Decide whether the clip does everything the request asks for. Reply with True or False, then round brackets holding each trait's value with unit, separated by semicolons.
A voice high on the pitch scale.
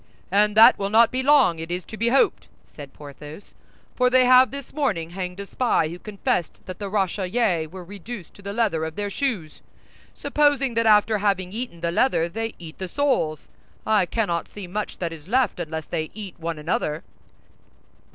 True (200 Hz)